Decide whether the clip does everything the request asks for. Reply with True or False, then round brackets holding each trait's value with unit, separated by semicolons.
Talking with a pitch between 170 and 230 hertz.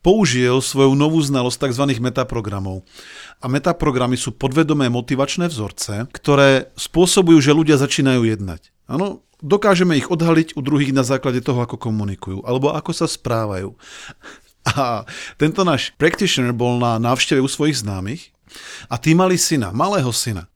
False (135 Hz)